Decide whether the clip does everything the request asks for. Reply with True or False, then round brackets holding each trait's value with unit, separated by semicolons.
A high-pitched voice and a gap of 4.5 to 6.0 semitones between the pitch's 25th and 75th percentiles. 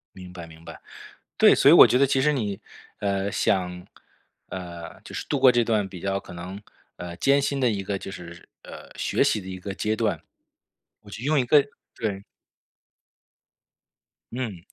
False (100 Hz; 5.1 semitones)